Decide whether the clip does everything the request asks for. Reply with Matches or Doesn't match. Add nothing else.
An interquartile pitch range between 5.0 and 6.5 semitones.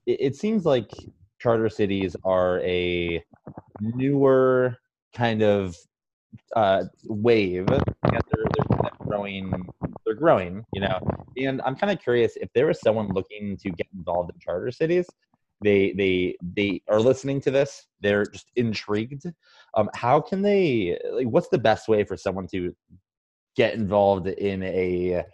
Matches